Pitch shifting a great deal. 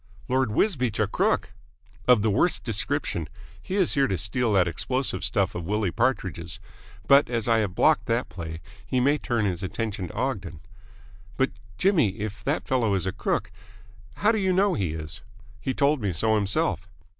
Yes: wide, 5.8 semitones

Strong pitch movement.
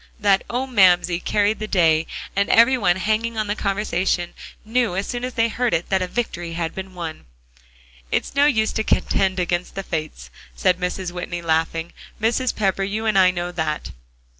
No: average, 3.9 semitones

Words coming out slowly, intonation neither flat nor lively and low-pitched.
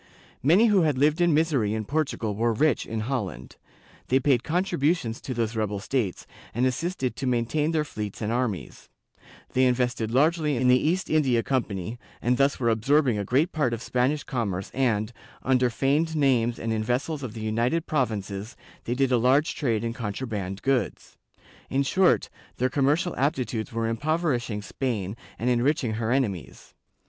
No: average, 170 wpm; average, 4.4 semitones; low, 125 Hz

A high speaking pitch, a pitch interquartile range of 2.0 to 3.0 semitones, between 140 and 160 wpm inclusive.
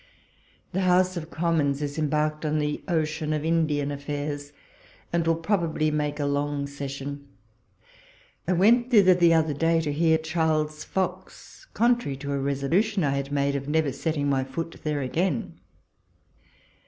No: medium, 155 Hz; average, 2.7 semitones; average, 155 wpm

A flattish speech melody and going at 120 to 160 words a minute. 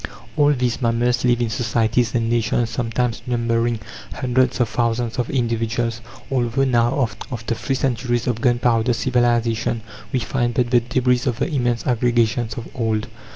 Yes: narrow, 1.2 semitones; average, 155 wpm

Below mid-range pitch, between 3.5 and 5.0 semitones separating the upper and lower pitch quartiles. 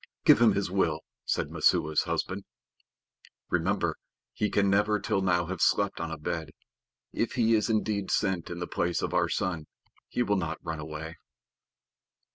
Yes: very low, 95 Hz; average, 4.0 semitones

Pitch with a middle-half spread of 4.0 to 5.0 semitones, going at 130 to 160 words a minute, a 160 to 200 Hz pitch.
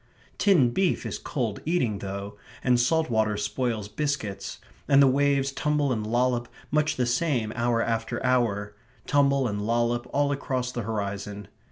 No: average, 4.4 semitones; average, 155 wpm; low, 120 Hz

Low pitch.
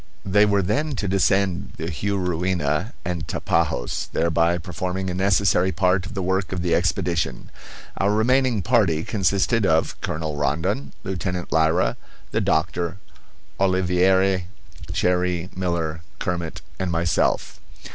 Yes: very low, 90 Hz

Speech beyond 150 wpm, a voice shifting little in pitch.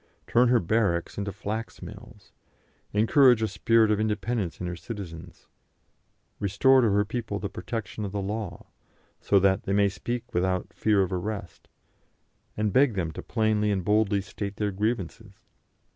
Yes: average, 160 wpm; narrow, 2.3 semitones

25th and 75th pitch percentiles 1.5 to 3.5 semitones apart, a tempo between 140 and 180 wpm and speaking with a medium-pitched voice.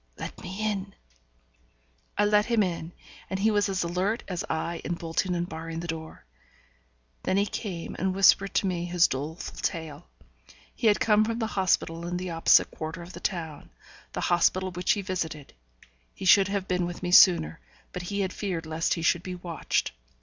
No: average, 2.8 semitones; average, 190 wpm; medium, 180 Hz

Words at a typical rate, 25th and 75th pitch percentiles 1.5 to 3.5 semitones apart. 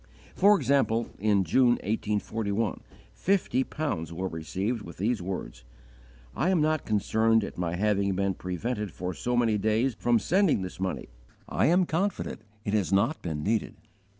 No: average, 155 wpm; average, 4.7 semitones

